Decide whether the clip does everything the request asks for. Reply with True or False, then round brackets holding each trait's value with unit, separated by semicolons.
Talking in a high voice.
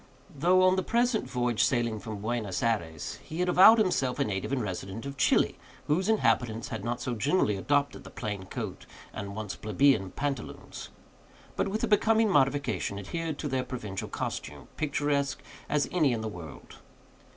False (130 Hz)